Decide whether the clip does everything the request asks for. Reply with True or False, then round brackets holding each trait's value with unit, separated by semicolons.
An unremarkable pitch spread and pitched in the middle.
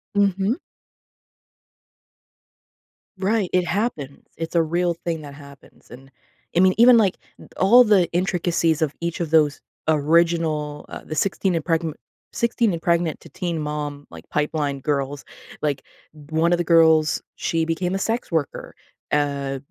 True (3.2 semitones; 165 Hz)